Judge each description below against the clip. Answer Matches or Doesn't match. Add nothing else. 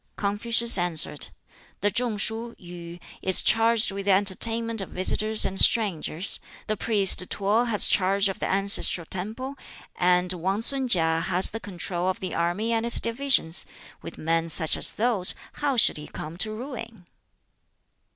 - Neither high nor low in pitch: Doesn't match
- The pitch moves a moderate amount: Matches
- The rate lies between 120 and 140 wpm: Doesn't match